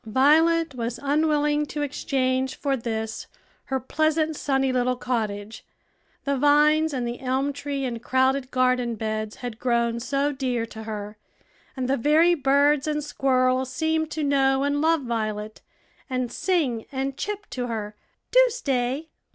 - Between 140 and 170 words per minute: Yes, average, 150 wpm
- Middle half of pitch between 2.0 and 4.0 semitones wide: Yes, average, 3.5 semitones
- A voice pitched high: Yes, very high, 265 Hz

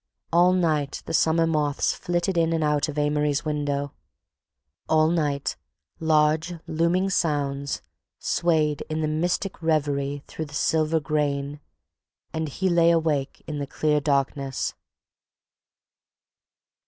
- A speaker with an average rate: No, slow, 115 wpm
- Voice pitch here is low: No, medium, 155 Hz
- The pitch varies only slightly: Yes, narrow, 2.2 semitones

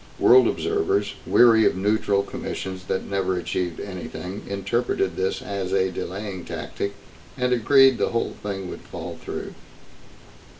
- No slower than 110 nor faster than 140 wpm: Yes, slow, 135 wpm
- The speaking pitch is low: Yes, low, 100 Hz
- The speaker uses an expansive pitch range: No, average, 3.9 semitones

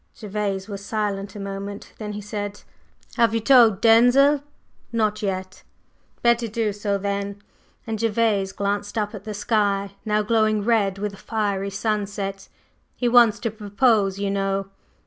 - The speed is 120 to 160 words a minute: Yes, average, 150 wpm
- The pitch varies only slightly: Yes, narrow, 2.0 semitones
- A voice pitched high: Yes, high, 205 Hz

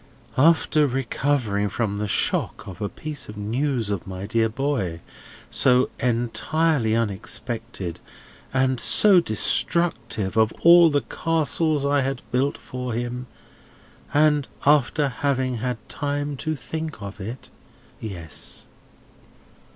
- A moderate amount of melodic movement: Yes, average, 4.9 semitones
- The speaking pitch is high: No, low, 125 Hz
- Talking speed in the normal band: No, slow, 120 wpm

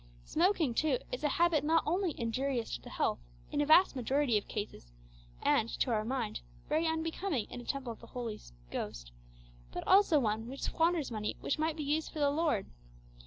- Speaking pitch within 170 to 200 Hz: No, very high, 280 Hz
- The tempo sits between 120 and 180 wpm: No, average, 195 wpm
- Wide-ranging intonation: Yes, wide, 5.7 semitones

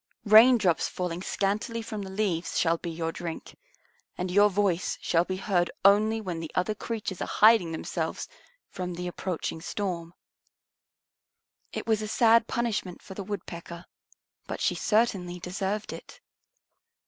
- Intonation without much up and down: No, average, 3.3 semitones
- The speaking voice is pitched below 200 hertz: Yes, high, 190 Hz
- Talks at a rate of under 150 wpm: Yes, average, 140 wpm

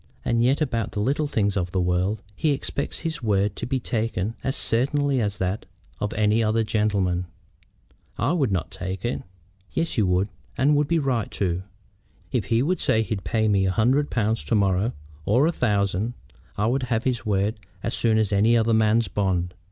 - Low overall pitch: Yes, low, 110 Hz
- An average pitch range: Yes, average, 3.8 semitones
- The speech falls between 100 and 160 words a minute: No, average, 195 wpm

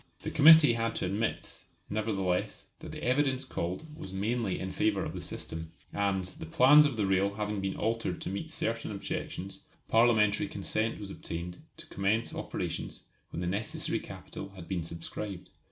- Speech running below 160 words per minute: No, average, 170 wpm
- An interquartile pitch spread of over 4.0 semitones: No, average, 3.4 semitones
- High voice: No, low, 100 Hz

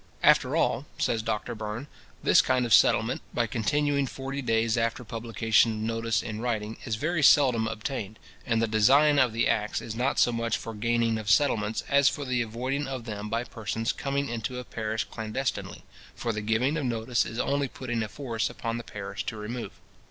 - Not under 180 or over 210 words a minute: Yes, average, 195 wpm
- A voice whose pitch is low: Yes, low, 115 Hz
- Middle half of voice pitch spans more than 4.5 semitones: No, average, 2.7 semitones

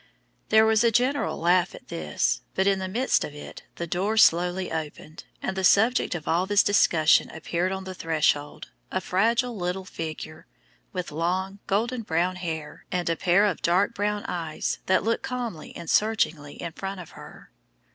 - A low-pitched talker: No, medium, 185 Hz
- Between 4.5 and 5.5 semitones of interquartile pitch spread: No, average, 3.8 semitones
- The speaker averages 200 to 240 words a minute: No, average, 175 wpm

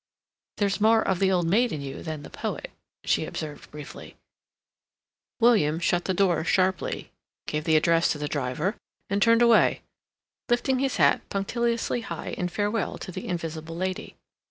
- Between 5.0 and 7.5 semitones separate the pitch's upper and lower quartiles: Yes, wide, 5.4 semitones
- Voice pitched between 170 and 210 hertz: Yes, medium, 185 Hz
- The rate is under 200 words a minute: Yes, average, 160 wpm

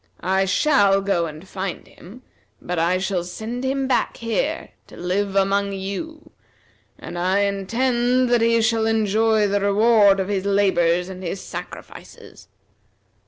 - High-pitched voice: Yes, high, 200 Hz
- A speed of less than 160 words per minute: Yes, average, 145 wpm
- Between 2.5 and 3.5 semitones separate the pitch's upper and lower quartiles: Yes, average, 3.2 semitones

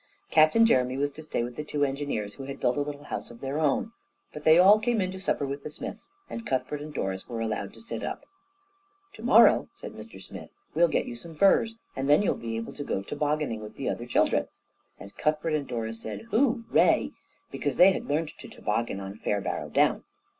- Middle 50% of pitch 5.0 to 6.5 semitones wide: Yes, average, 5.3 semitones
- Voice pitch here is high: No, medium, 145 Hz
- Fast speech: Yes, fast, 220 wpm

